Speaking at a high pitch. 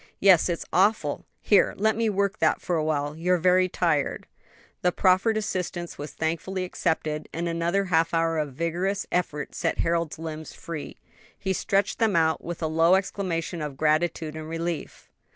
No: medium, 170 Hz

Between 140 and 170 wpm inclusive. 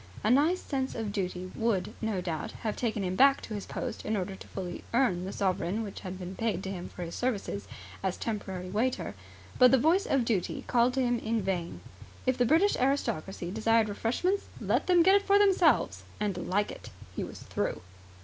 No: fast, 205 wpm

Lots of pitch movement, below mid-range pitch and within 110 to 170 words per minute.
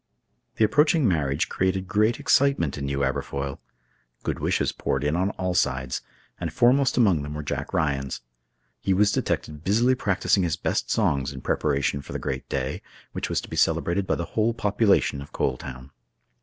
No: wide, 7.0 semitones; very low, 85 Hz; average, 180 wpm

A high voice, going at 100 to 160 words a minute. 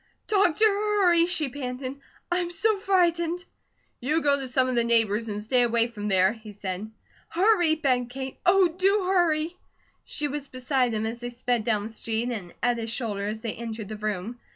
No: very high, 250 Hz; average, 190 wpm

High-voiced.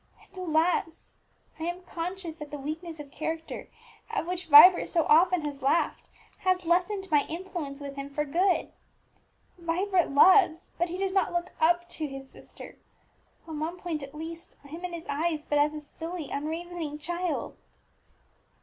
Yes: very high, 330 Hz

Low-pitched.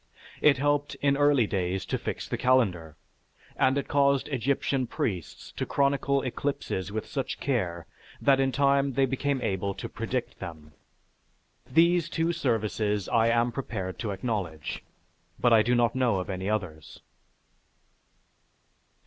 Yes: low, 120 Hz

